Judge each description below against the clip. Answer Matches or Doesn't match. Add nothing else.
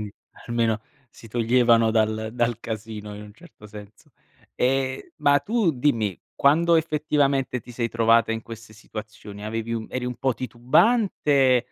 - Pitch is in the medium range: Doesn't match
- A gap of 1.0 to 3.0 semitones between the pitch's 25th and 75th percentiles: Doesn't match